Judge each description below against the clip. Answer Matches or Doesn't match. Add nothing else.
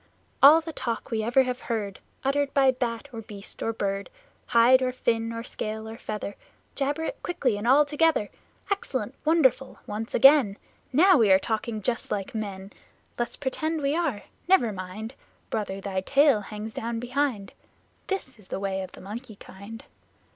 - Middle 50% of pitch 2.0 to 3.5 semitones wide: Doesn't match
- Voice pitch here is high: Matches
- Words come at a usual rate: Matches